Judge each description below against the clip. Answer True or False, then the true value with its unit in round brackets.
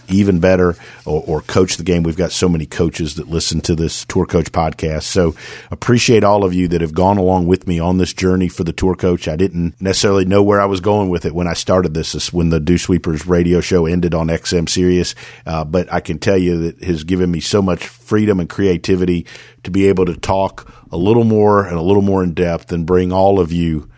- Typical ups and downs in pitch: False (2.3 semitones)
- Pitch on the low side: True (90 Hz)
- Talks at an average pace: False (240 wpm)